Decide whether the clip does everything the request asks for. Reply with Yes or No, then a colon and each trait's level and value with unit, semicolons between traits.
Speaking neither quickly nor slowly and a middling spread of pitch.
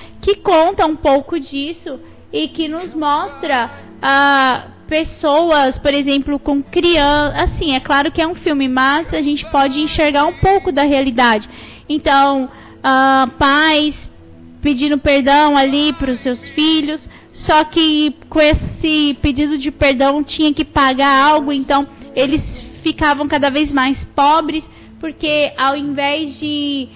No: average, 140 wpm; narrow, 1.9 semitones